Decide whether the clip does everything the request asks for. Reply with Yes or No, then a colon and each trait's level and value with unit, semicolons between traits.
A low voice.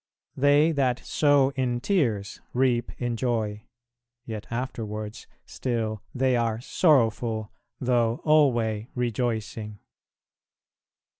Yes: low, 120 Hz